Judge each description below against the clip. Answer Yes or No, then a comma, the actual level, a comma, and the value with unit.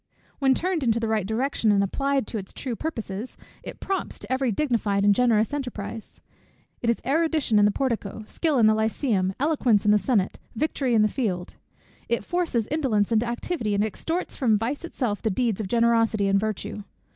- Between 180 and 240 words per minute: Yes, average, 190 wpm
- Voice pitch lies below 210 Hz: No, high, 230 Hz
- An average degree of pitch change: Yes, average, 4.4 semitones